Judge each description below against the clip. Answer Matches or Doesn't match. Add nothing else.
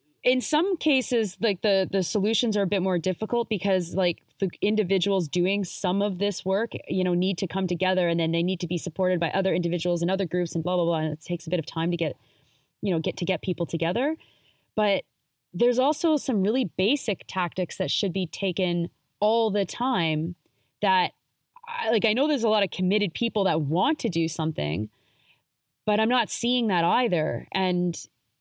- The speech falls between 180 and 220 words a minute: Matches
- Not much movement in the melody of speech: Doesn't match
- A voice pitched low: Doesn't match